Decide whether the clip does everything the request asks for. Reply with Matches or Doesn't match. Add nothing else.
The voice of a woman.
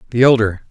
Doesn't match